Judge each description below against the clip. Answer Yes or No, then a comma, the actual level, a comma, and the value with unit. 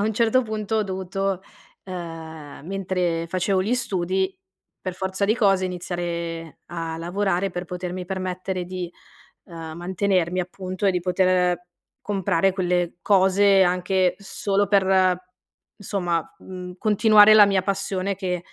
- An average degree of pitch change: No, narrow, 1.8 semitones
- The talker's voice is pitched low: No, medium, 185 Hz